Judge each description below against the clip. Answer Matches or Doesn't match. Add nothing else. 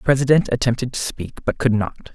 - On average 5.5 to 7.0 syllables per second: Matches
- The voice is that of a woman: Doesn't match